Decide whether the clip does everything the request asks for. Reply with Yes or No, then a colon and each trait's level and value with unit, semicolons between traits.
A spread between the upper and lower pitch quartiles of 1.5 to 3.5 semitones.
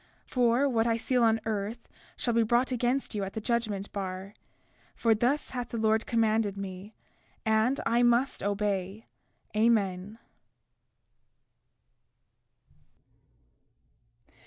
Yes: average, 2.8 semitones